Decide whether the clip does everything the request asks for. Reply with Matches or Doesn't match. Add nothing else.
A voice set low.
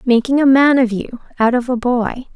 Doesn't match